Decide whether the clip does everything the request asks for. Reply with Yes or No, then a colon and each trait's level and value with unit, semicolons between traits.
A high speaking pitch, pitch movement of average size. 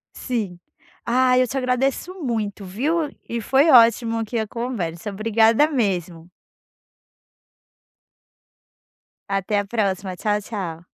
Yes: high, 225 Hz; average, 4.3 semitones